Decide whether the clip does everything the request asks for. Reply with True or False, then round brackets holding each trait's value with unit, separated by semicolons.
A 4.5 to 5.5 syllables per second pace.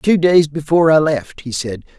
True (5.0 syllables/s)